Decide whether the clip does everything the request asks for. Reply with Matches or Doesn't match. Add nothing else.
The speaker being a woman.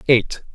Doesn't match